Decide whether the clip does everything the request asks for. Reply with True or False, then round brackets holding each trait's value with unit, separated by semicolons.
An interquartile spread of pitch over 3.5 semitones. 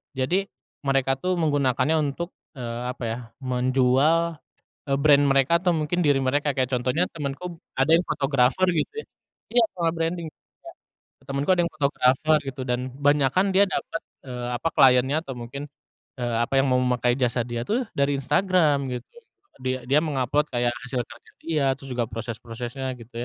True (3.9 semitones)